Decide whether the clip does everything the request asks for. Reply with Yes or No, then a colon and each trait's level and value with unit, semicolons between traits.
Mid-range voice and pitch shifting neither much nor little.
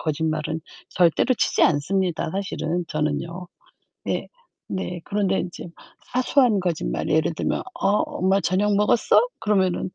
Yes: medium, 180 Hz; average, 3.7 semitones